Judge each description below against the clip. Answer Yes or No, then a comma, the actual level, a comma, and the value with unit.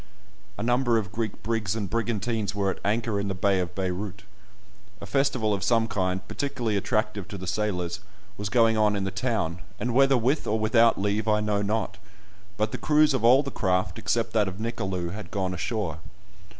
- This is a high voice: No, low, 105 Hz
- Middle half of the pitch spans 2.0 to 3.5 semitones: Yes, average, 3.0 semitones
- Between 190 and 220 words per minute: Yes, average, 195 wpm